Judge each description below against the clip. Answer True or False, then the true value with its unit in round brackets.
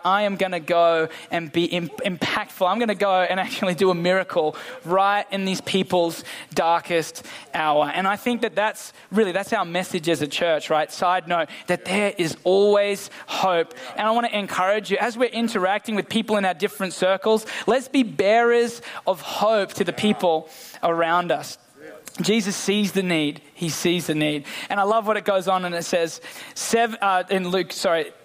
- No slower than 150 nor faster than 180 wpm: False (190 wpm)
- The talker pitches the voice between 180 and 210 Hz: True (190 Hz)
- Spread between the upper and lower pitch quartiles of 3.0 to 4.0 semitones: True (3.3 semitones)